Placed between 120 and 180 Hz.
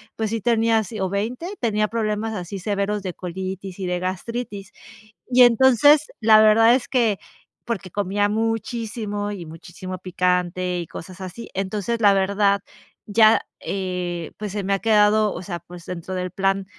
No: high, 200 Hz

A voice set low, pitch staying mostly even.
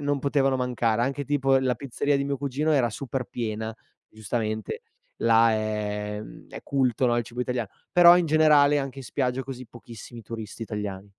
No: low, 125 Hz; average, 3.8 semitones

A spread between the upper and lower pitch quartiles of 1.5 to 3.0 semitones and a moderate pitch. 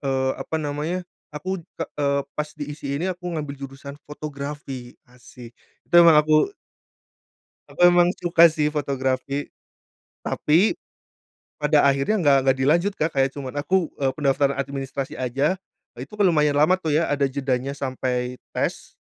Yes: narrow, 2.6 semitones; medium, 145 Hz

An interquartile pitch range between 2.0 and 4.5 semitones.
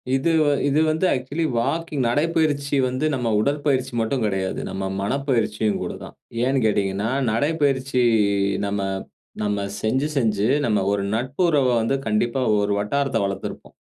No: average, 4.9 semitones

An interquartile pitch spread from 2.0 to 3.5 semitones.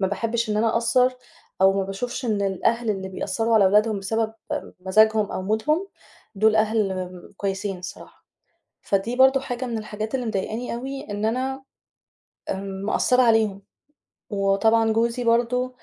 Yes: average, 3.2 semitones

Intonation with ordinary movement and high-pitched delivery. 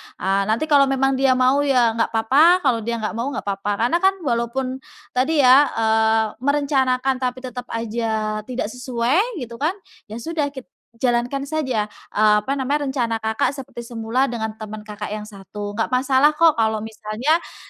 Yes: average, 3.7 semitones; very high, 250 Hz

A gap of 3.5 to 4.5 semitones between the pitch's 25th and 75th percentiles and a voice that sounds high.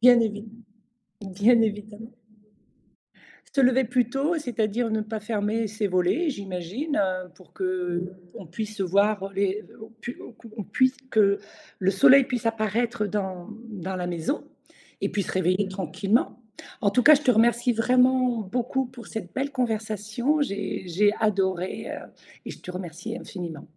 Yes: average, 4.2 semitones; high, 215 Hz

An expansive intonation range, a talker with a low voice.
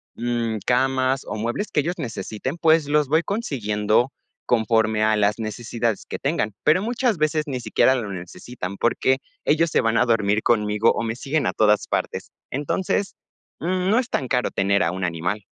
Yes: wide, 5.8 semitones; low, 120 Hz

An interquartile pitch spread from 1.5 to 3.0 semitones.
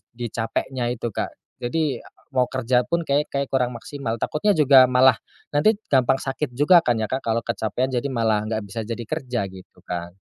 No: average, 3.4 semitones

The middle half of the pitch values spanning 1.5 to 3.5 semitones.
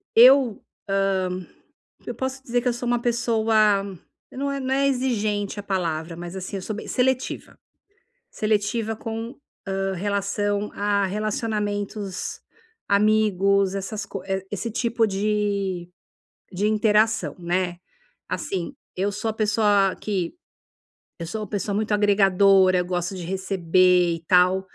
Yes: narrow, 2.5 semitones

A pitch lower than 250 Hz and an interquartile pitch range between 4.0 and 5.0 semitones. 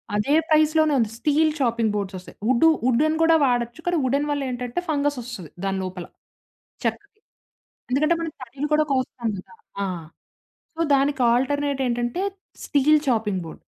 No: very high, 265 Hz; average, 4.5 semitones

